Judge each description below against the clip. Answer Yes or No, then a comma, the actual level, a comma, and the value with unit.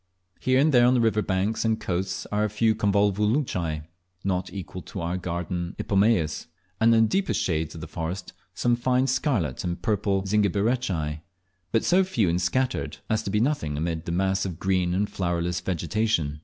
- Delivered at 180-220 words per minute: Yes, average, 185 wpm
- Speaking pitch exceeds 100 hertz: No, very low, 95 Hz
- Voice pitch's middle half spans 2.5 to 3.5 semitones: No, average, 4.4 semitones